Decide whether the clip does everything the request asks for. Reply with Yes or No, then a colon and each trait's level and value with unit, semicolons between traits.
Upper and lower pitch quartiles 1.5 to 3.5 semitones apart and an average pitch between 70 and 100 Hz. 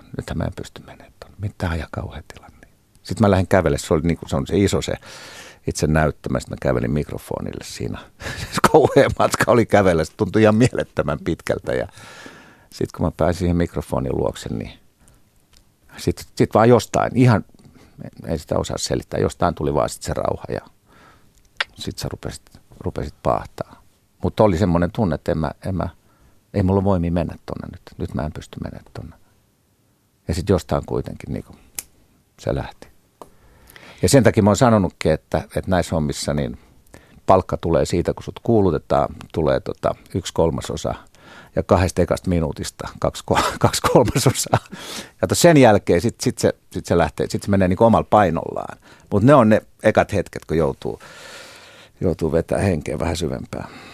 No: average, 4.2 semitones; very low, 95 Hz